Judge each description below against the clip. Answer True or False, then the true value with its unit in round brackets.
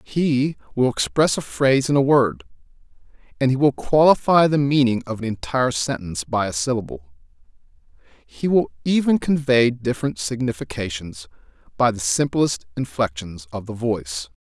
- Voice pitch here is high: False (120 Hz)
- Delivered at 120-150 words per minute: True (140 wpm)